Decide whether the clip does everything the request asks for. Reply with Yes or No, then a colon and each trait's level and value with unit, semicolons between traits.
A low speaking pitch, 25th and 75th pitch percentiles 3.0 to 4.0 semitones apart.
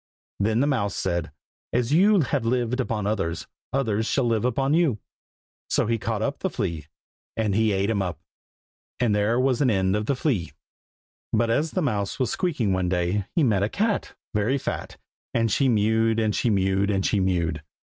No: low, 110 Hz; average, 4.4 semitones